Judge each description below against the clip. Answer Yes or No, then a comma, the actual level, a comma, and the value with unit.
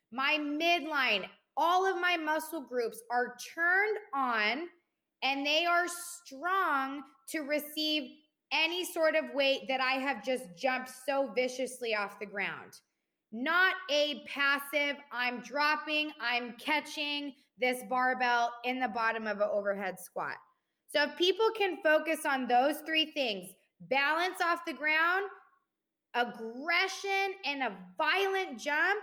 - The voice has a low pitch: No, very high, 285 Hz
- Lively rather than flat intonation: No, average, 4.8 semitones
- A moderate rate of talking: No, slow, 130 wpm